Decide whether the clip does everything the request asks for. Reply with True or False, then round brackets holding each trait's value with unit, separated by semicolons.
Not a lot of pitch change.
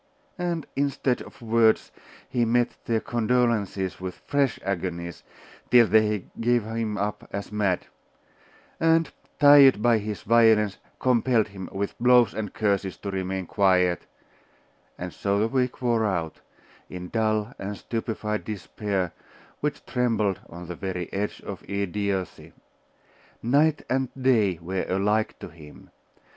False (3.8 semitones)